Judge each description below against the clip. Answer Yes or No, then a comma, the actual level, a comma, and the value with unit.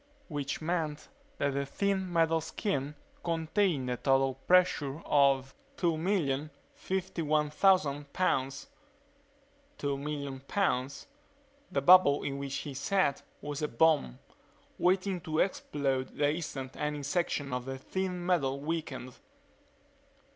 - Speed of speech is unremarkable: No, slow, 110 wpm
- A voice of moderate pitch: Yes, medium, 150 Hz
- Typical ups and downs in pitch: Yes, average, 4.1 semitones